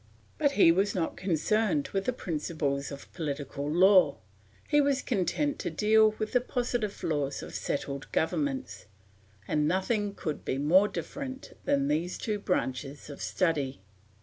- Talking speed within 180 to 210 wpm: No, average, 150 wpm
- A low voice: No, medium, 185 Hz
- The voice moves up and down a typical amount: No, wide, 6.9 semitones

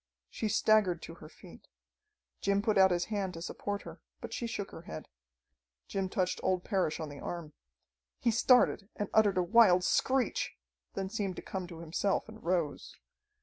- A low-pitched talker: No, high, 190 Hz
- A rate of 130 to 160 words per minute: No, average, 180 wpm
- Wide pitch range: No, average, 3.3 semitones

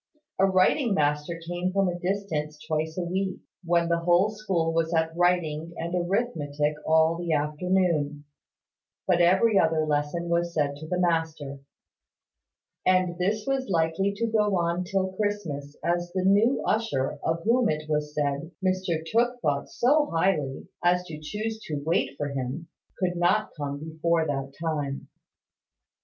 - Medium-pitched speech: Yes, medium, 170 Hz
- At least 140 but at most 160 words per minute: Yes, average, 155 wpm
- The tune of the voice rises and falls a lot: No, average, 3.6 semitones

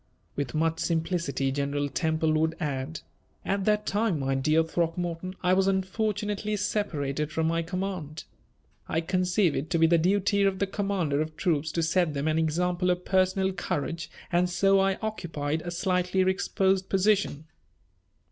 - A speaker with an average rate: Yes, average, 155 wpm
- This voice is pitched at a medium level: Yes, medium, 175 Hz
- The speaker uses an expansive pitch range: No, average, 3.4 semitones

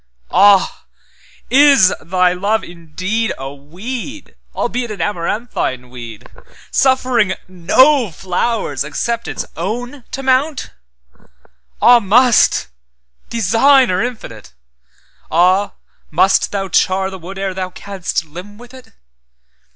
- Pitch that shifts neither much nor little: No, wide, 7.7 semitones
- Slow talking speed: Yes, slow, 90 wpm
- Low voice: No, high, 190 Hz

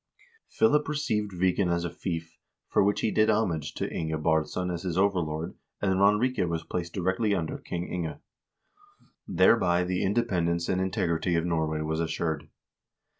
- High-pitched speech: No, very low, 90 Hz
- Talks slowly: No, average, 155 wpm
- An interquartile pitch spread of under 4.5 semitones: Yes, average, 3.2 semitones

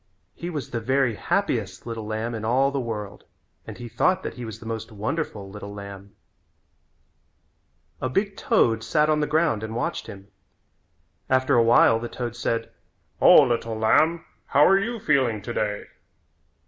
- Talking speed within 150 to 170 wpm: Yes, average, 165 wpm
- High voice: No, low, 115 Hz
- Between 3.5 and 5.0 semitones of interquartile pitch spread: Yes, average, 4.1 semitones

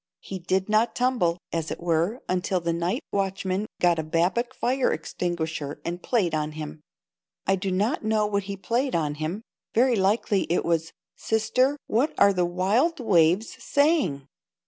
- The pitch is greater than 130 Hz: Yes, high, 190 Hz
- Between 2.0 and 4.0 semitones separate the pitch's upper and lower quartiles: No, average, 4.8 semitones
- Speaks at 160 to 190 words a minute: Yes, average, 165 wpm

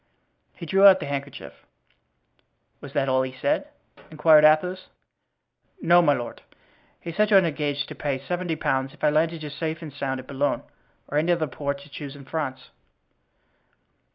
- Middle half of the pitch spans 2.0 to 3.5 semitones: Yes, average, 3.1 semitones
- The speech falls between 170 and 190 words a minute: Yes, average, 180 wpm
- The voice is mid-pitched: Yes, medium, 150 Hz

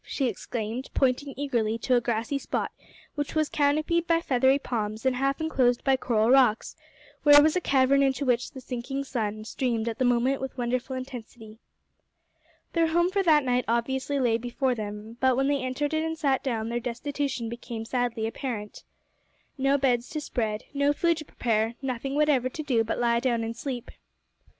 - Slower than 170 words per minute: No, average, 185 wpm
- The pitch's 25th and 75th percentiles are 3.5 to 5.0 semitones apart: No, average, 3.1 semitones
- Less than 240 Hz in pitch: No, very high, 255 Hz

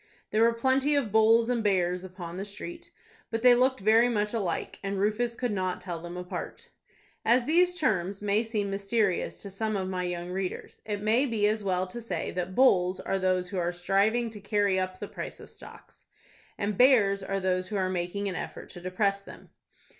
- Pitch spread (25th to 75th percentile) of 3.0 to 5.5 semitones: Yes, average, 3.5 semitones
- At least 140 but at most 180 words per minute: No, fast, 205 wpm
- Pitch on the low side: No, high, 200 Hz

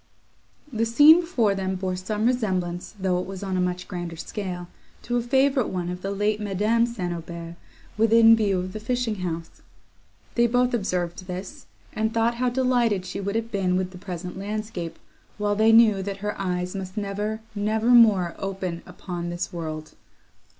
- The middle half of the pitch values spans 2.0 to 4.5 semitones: Yes, average, 3.8 semitones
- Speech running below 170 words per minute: No, average, 180 wpm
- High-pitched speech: Yes, high, 200 Hz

